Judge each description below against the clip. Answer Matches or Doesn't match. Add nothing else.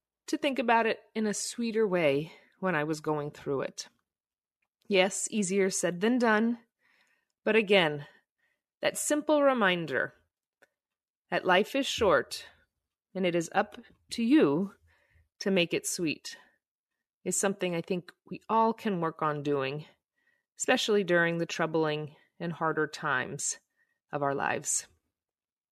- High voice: Matches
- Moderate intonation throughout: Doesn't match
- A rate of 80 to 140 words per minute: Matches